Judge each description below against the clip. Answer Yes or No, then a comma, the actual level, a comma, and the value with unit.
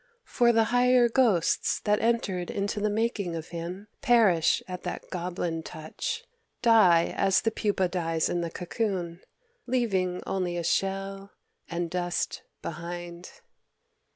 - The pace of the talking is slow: Yes, slow, 130 wpm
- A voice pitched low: No, medium, 185 Hz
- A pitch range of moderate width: Yes, average, 4.4 semitones